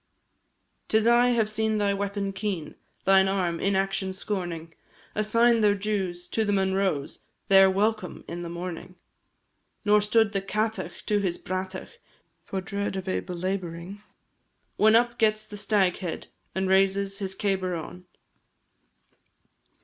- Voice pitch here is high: Yes, high, 195 Hz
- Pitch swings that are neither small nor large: No, narrow, 2.2 semitones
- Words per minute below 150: Yes, slow, 135 wpm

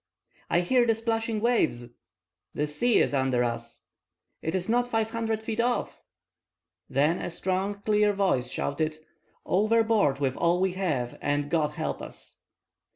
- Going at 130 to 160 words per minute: Yes, average, 150 wpm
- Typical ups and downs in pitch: No, wide, 7.5 semitones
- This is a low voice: No, medium, 185 Hz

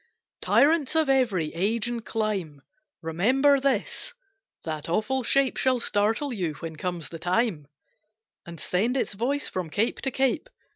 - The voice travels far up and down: Yes, wide, 7.4 semitones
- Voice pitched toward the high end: Yes, high, 220 Hz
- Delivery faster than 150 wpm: No, average, 145 wpm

